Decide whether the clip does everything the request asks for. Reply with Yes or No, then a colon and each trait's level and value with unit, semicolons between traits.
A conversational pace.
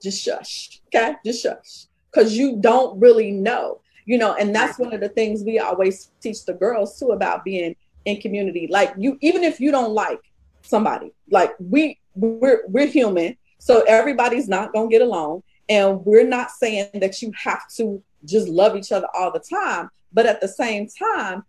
Yes: average, 185 wpm